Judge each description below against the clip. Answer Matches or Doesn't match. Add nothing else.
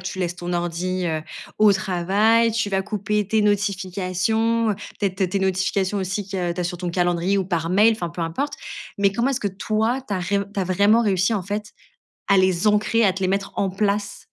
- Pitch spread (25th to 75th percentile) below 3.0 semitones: Matches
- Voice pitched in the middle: Doesn't match